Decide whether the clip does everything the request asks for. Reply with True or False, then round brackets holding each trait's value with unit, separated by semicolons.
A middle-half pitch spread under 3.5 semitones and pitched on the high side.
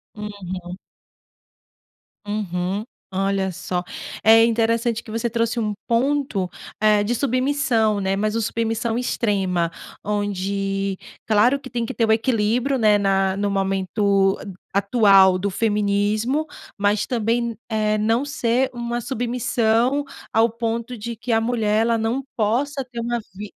True (2.9 semitones; 220 Hz)